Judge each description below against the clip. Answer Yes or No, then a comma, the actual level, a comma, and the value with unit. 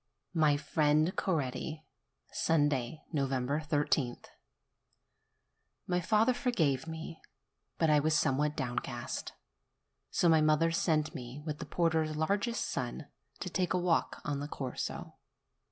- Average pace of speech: No, slow, 120 wpm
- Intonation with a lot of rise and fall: No, narrow, 2.4 semitones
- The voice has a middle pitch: Yes, medium, 155 Hz